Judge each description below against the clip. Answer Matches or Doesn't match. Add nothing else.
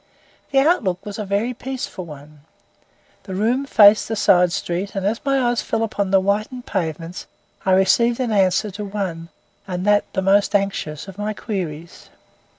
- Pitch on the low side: Doesn't match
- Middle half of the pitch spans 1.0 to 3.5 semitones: Matches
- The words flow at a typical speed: Matches